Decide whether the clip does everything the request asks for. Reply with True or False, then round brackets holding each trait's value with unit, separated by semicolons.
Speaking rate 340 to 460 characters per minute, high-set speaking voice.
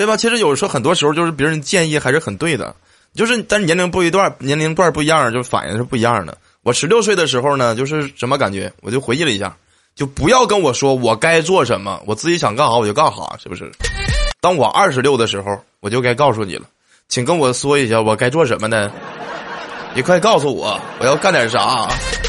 False (345 characters per minute; 140 Hz)